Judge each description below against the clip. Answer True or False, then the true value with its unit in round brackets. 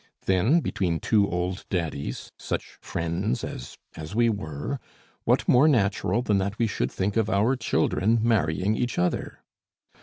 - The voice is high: False (100 Hz)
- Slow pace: False (150 wpm)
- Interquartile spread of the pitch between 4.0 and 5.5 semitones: True (4.4 semitones)